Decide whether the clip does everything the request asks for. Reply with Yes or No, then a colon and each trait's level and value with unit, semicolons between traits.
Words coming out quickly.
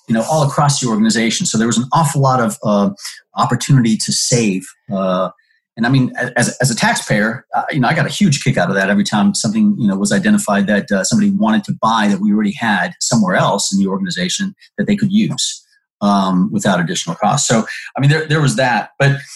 Yes: fast, 230 wpm